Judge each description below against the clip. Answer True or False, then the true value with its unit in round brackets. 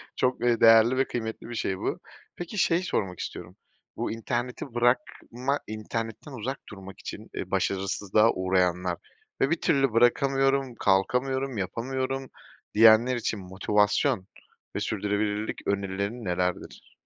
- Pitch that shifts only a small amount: False (4.5 semitones)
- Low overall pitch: True (115 Hz)